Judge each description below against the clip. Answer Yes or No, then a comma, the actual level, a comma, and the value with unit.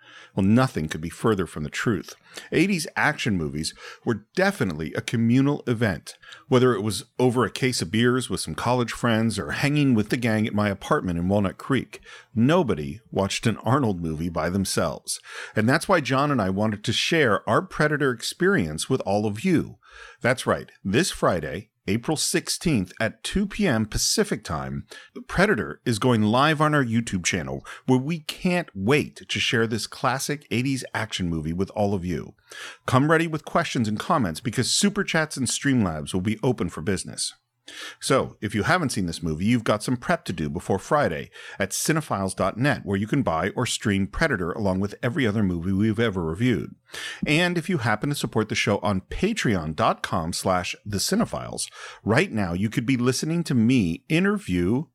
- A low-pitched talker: Yes, low, 115 Hz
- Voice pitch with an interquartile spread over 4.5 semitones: Yes, wide, 5.5 semitones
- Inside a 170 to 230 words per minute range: Yes, average, 180 wpm